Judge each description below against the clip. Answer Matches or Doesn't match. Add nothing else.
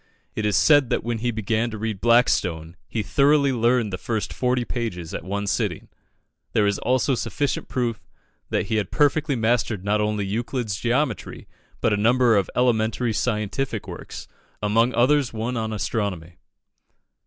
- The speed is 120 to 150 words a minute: Doesn't match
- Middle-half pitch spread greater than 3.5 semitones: Doesn't match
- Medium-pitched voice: Doesn't match